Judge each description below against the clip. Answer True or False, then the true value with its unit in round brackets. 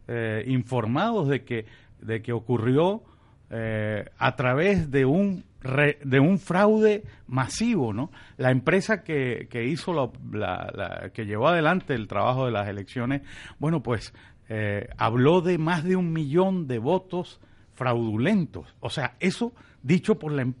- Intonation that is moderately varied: False (7.3 semitones)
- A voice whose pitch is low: True (130 Hz)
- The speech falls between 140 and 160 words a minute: True (155 wpm)